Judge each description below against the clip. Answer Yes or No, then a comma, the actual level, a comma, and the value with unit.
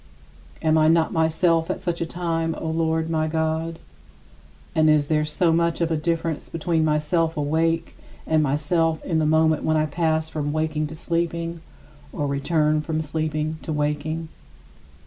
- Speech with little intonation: Yes, narrow, 1.2 semitones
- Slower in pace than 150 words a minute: No, average, 165 wpm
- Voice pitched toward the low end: No, medium, 160 Hz